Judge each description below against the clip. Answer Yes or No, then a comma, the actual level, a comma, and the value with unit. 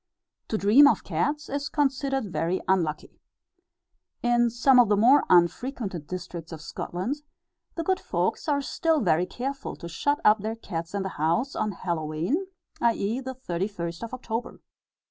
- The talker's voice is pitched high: Yes, high, 220 Hz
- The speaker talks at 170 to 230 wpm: No, average, 155 wpm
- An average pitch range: No, wide, 7.4 semitones